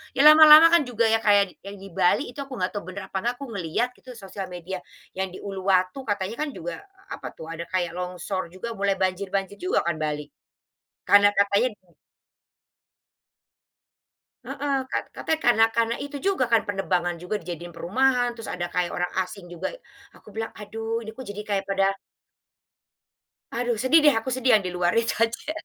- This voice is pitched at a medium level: No, high, 205 Hz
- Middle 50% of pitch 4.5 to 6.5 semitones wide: Yes, average, 4.8 semitones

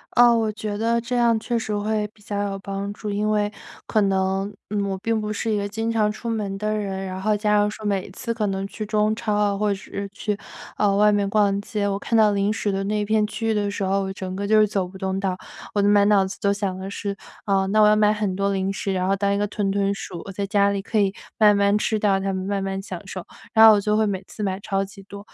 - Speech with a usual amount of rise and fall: No, narrow, 1.4 semitones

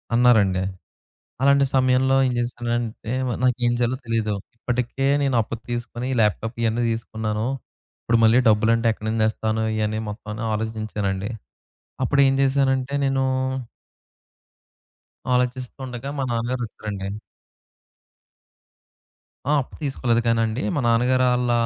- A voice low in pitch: Yes, low, 120 Hz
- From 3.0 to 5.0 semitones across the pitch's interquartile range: No, narrow, 2.6 semitones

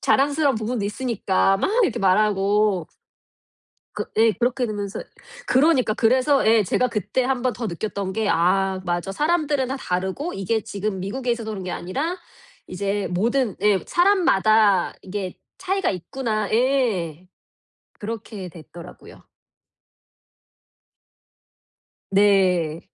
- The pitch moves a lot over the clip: No, average, 4.9 semitones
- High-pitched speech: Yes, high, 215 Hz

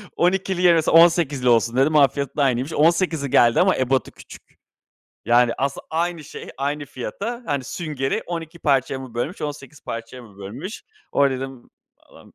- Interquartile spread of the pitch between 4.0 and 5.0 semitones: Yes, average, 4.4 semitones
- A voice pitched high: No, medium, 140 Hz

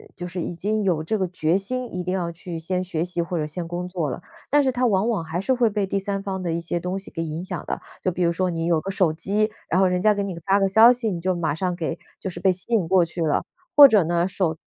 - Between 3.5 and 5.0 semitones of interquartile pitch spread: No, average, 2.7 semitones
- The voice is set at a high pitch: No, medium, 180 Hz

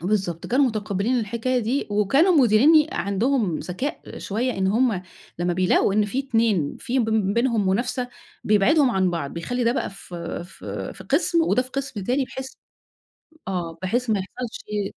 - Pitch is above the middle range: Yes, high, 220 Hz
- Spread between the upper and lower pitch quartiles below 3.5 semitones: No, average, 5.0 semitones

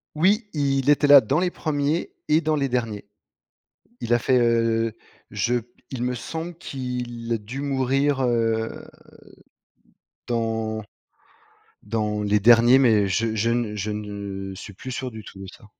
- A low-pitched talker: Yes, low, 120 Hz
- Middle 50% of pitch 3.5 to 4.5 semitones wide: Yes, average, 3.8 semitones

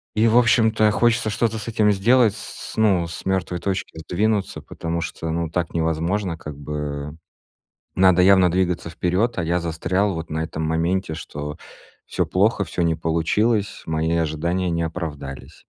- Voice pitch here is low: Yes, very low, 85 Hz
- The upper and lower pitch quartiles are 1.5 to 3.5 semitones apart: No, average, 4.2 semitones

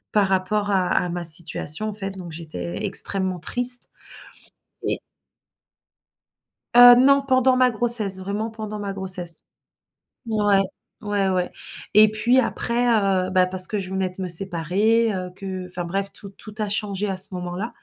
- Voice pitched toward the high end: Yes, high, 195 Hz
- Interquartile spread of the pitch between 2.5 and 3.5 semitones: Yes, average, 2.8 semitones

